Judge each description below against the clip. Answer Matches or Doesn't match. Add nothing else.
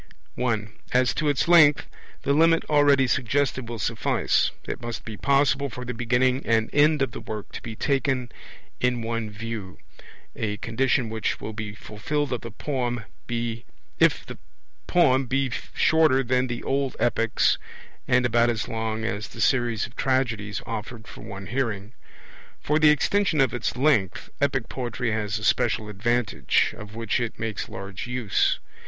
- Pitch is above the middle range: Doesn't match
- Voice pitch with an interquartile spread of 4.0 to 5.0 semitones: Doesn't match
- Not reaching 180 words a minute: Matches